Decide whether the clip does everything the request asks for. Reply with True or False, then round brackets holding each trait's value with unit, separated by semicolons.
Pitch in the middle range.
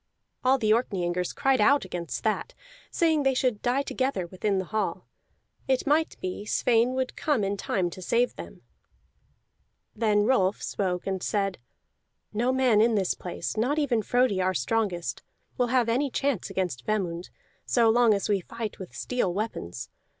False (220 Hz)